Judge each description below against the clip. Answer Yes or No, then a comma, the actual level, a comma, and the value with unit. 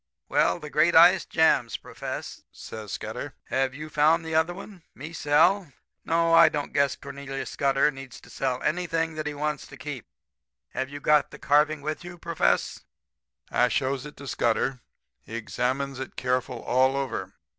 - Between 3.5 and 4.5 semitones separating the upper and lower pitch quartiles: No, average, 2.8 semitones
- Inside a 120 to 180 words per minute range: Yes, average, 170 wpm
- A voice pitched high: No, medium, 140 Hz